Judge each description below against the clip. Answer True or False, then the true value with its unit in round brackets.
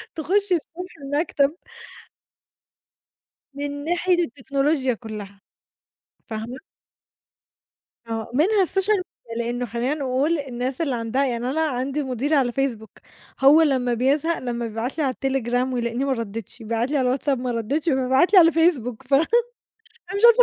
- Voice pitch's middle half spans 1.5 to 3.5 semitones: False (4.4 semitones)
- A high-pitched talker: True (265 Hz)